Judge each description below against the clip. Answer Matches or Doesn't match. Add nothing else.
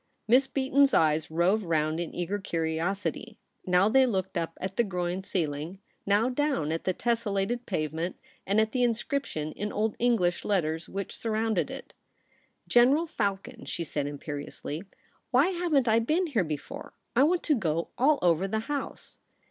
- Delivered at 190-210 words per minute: Doesn't match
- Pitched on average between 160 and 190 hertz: Doesn't match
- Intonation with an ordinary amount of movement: Doesn't match